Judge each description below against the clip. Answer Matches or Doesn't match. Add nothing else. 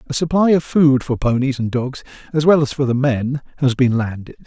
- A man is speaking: Matches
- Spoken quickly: Matches